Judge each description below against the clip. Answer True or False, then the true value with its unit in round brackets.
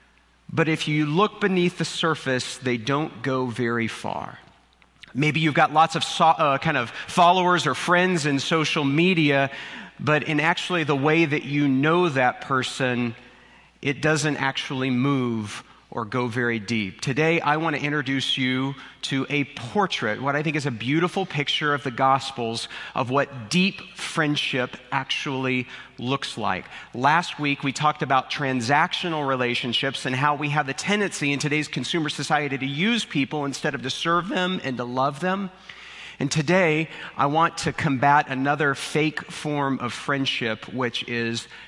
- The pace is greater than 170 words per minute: False (165 wpm)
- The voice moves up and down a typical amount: True (3.5 semitones)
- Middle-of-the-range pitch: True (145 Hz)